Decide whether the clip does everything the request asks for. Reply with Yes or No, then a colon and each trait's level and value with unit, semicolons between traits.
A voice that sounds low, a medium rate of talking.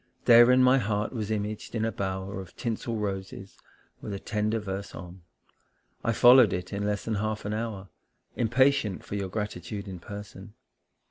Yes: low, 105 Hz; average, 170 wpm